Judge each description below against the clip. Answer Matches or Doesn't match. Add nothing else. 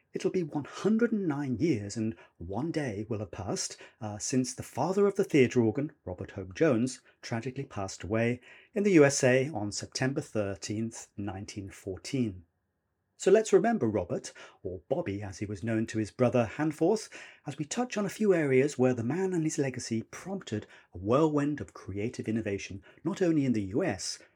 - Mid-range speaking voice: Doesn't match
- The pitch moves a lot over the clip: Matches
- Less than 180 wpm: Matches